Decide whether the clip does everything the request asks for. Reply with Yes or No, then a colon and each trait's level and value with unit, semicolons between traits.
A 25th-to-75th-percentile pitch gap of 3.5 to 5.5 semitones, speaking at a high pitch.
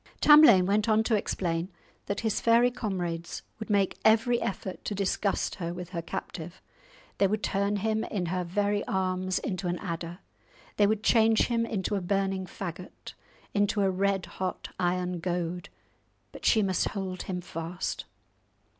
No: average, 2.9 semitones; high, 195 Hz